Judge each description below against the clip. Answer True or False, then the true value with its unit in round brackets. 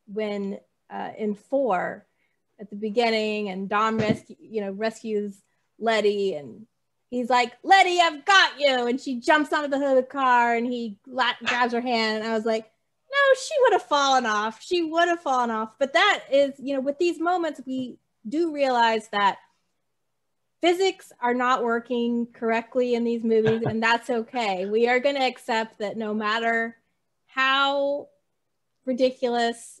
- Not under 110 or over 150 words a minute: False (170 wpm)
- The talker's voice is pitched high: True (240 Hz)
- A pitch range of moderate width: True (3.9 semitones)